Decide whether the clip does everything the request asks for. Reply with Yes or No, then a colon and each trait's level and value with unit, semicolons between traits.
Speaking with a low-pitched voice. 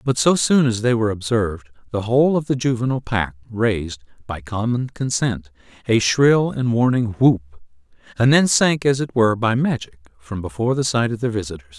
Yes: low, 115 Hz